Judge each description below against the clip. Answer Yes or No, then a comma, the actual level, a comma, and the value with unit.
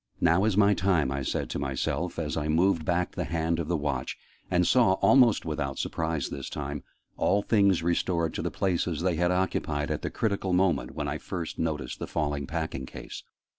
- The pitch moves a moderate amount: Yes, average, 4.1 semitones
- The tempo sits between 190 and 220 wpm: Yes, fast, 205 wpm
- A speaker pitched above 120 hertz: No, very low, 85 Hz